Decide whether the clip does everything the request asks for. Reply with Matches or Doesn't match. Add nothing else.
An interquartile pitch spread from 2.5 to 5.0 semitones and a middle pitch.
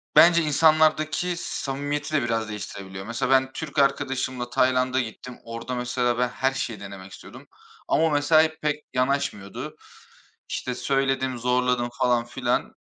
Doesn't match